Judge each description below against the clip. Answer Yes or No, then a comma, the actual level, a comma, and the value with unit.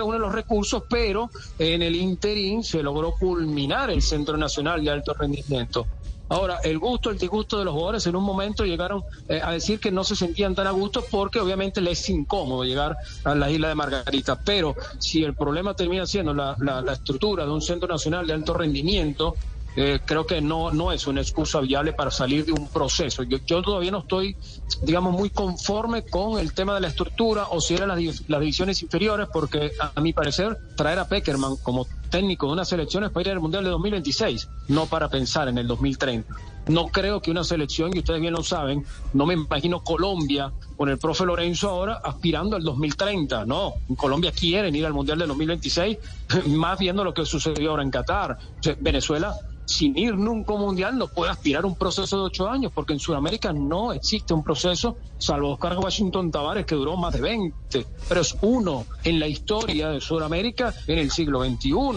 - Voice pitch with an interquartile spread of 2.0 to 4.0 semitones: No, average, 4.7 semitones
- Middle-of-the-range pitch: Yes, medium, 165 Hz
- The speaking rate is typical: No, fast, 205 wpm